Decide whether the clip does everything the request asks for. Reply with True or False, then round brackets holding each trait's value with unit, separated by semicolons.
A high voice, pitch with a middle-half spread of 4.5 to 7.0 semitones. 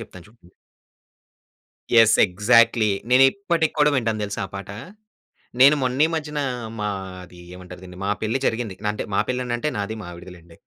False (110 Hz; 5.2 semitones)